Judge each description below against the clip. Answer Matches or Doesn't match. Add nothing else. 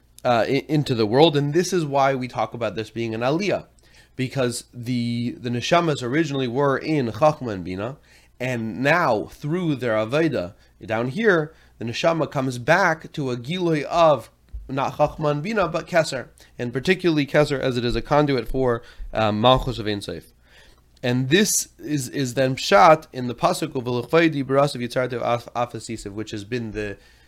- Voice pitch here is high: Doesn't match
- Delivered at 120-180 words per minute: Matches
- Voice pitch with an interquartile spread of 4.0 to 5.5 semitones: Matches